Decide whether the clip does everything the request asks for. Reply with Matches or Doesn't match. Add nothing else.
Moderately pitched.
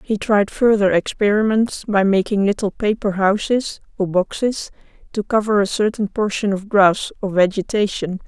Doesn't match